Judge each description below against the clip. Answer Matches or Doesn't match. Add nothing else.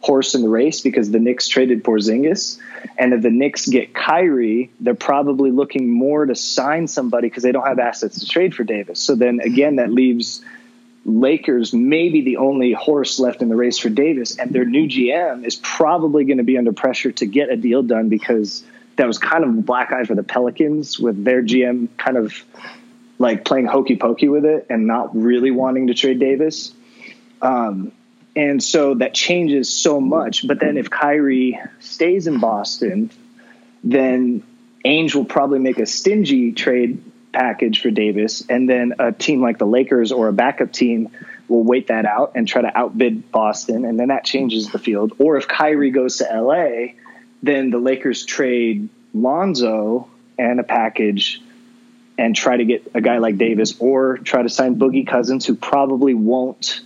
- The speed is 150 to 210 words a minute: Matches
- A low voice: Matches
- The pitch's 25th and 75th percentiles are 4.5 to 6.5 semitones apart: Matches